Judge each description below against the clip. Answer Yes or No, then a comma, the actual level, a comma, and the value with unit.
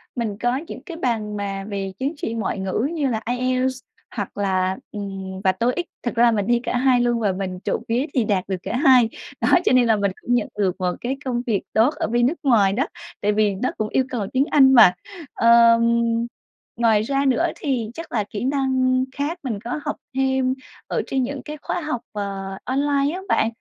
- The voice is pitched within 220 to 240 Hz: Yes, high, 235 Hz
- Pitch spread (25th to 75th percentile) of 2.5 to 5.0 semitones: Yes, average, 4.3 semitones